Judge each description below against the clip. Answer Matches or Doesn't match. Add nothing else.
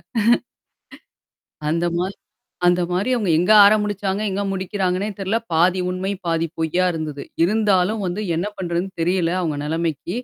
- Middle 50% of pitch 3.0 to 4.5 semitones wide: Doesn't match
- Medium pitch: Matches